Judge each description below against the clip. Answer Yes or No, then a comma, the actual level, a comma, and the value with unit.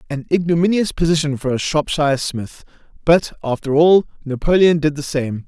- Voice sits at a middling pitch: Yes, medium, 155 Hz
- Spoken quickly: No, average, 165 wpm